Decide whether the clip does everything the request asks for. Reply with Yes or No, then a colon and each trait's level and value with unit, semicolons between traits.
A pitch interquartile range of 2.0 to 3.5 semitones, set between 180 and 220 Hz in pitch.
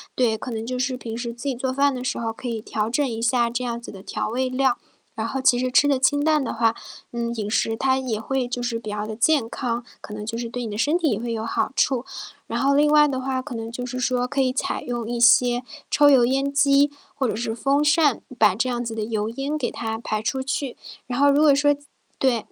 No: average, 3.0 semitones; high, 245 Hz